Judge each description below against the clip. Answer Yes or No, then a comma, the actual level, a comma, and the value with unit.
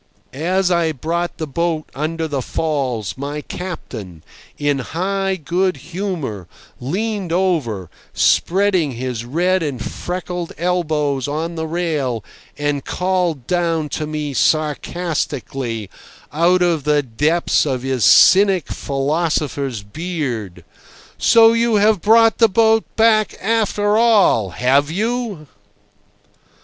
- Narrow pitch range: No, average, 5.0 semitones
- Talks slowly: Yes, slow, 115 wpm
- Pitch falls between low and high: Yes, medium, 160 Hz